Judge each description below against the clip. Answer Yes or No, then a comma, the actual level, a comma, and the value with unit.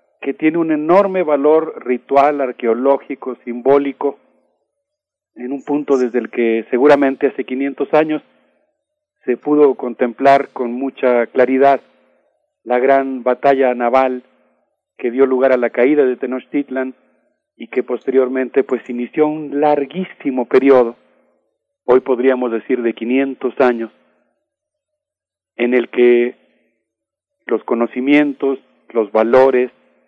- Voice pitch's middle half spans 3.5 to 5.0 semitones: No, average, 2.8 semitones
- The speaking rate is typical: No, slow, 115 wpm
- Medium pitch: No, low, 130 Hz